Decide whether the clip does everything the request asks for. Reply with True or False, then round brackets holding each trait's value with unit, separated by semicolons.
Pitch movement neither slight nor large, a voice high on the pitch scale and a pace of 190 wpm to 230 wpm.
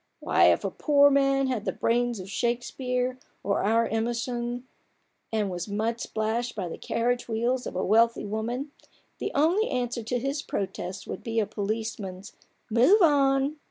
False (3.0 semitones; 235 Hz; 165 wpm)